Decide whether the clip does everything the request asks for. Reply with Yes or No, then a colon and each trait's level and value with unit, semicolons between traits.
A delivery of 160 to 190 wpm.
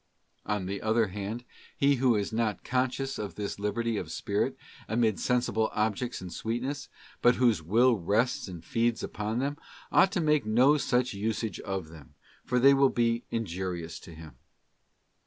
Yes: average, 170 wpm